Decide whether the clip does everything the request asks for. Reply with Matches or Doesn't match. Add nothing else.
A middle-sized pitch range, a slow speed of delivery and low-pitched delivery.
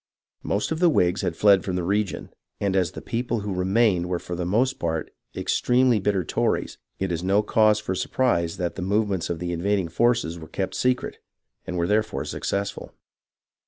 Doesn't match